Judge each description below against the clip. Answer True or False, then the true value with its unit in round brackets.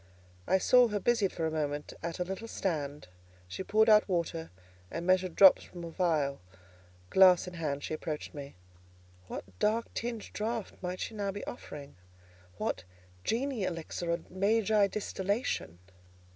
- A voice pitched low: False (185 Hz)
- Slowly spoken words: False (155 wpm)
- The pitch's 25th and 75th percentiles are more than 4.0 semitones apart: True (4.7 semitones)